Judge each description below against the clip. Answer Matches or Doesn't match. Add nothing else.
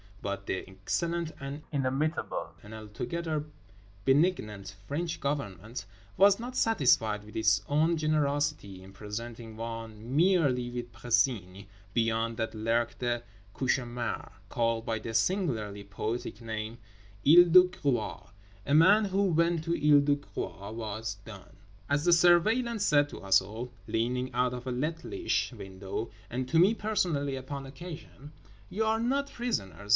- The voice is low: Matches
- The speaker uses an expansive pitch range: Matches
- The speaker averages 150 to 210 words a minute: Doesn't match